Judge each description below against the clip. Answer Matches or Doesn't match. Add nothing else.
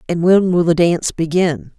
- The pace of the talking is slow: Doesn't match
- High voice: Doesn't match